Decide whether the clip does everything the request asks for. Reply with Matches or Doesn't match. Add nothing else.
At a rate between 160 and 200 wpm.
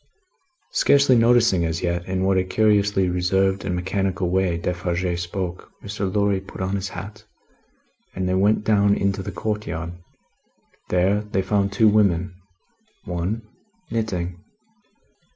Doesn't match